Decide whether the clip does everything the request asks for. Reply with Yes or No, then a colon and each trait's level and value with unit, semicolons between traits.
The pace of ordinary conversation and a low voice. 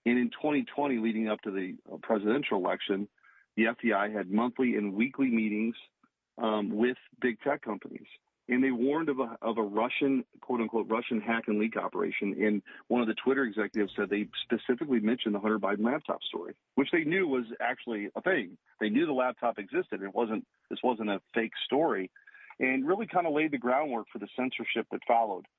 Yes: average, 190 wpm; low, 115 Hz